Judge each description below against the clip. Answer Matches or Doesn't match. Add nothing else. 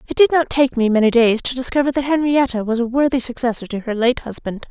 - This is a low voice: Doesn't match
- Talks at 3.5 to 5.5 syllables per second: Doesn't match